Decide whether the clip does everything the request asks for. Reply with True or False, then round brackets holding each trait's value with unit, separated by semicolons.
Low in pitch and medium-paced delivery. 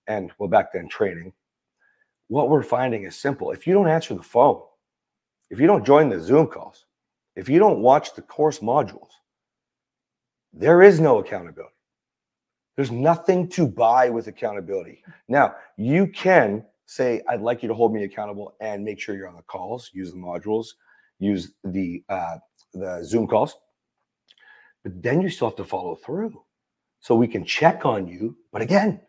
True (120 Hz; 170 wpm)